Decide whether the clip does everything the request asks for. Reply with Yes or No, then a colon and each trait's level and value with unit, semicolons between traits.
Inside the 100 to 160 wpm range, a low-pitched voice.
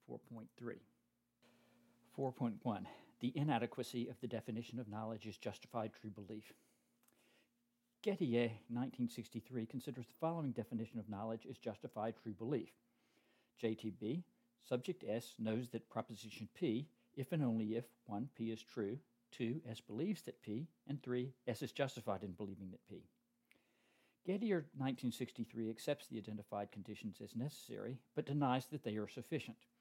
Yes: slow, 135 wpm; low, 120 Hz